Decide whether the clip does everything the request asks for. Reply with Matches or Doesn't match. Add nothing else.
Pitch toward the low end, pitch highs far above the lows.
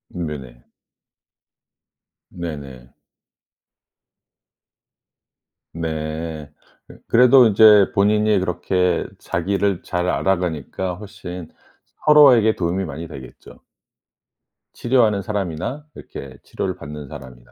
Doesn't match